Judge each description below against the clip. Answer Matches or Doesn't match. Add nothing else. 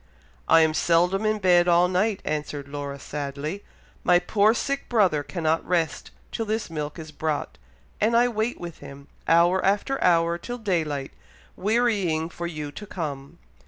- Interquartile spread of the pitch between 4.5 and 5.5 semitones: Matches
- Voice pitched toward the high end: Doesn't match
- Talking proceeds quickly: Doesn't match